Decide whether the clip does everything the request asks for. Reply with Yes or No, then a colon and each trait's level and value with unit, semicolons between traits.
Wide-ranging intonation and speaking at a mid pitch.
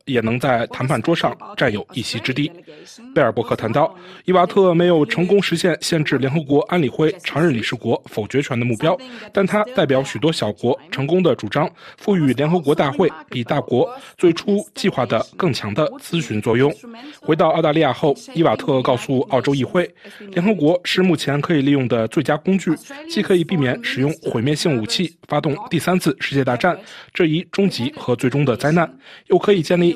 No: average, 5.0 semitones; medium, 160 Hz